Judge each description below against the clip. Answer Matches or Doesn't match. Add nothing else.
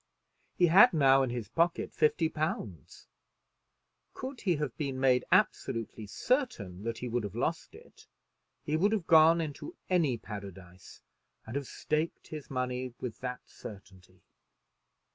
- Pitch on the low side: Matches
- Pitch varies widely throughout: Matches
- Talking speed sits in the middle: Matches